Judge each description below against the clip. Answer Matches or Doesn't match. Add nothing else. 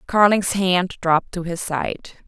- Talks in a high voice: Doesn't match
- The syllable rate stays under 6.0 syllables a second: Matches